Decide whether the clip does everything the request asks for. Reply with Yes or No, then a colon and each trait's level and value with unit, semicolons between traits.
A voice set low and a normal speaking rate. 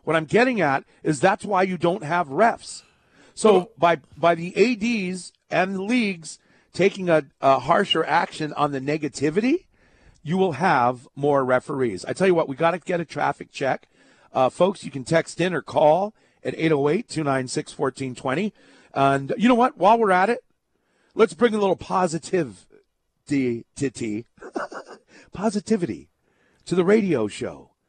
No: medium, 170 Hz; average, 155 wpm